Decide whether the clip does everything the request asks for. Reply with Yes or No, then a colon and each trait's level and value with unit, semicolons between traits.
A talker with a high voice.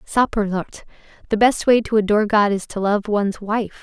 Yes: high, 210 Hz